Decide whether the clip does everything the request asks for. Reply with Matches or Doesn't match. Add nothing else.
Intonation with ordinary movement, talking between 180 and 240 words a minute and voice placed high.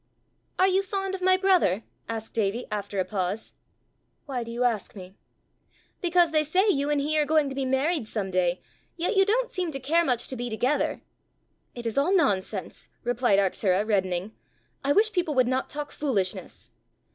Doesn't match